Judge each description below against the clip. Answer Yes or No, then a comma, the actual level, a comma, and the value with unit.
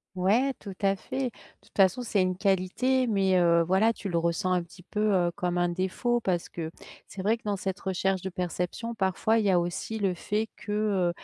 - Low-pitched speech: No, high, 190 Hz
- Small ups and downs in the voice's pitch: No, average, 3.1 semitones